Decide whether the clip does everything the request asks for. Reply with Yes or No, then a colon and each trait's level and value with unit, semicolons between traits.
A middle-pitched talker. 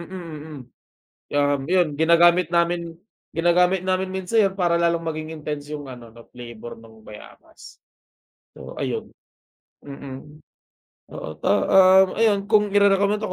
Yes: medium, 170 Hz